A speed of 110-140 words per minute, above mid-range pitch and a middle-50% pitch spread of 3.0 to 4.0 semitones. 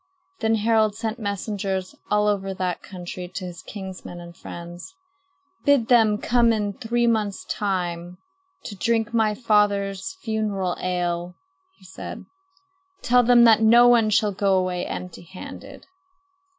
Yes: slow, 135 wpm; high, 205 Hz; average, 3.4 semitones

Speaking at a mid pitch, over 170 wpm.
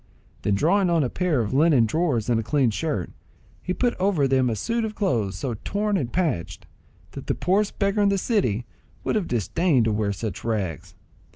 Yes: medium, 145 Hz; average, 200 wpm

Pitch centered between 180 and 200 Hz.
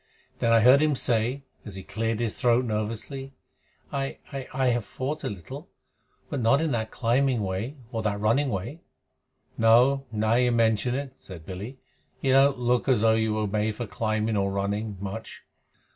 No: low, 115 Hz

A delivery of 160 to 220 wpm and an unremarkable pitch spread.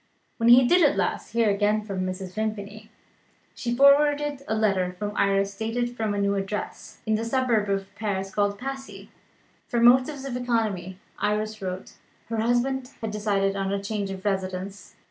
Yes: average, 170 wpm; average, 3.4 semitones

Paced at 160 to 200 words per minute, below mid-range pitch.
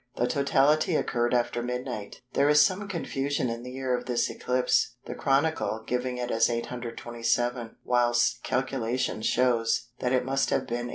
Yes: average, 165 wpm; low, 125 Hz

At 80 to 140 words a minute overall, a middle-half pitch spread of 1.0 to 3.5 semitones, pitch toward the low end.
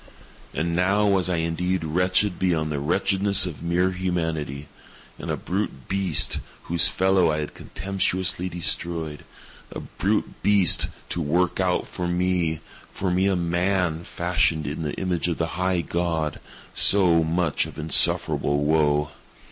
Yes: slow, 135 wpm; narrow, 2.5 semitones; very low, 85 Hz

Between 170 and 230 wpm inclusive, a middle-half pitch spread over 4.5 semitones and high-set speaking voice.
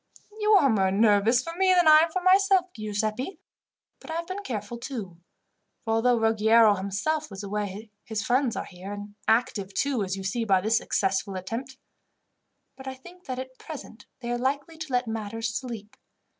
Yes: average, 185 wpm; wide, 5.4 semitones; high, 230 Hz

